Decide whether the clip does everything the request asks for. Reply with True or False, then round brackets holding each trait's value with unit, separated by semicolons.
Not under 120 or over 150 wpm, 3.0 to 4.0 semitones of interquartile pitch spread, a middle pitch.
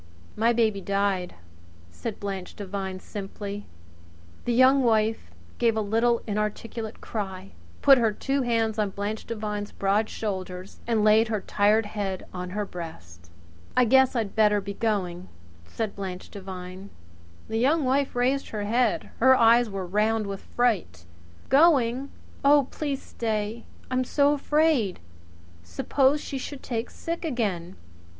False (140 wpm; 3.6 semitones; 215 Hz)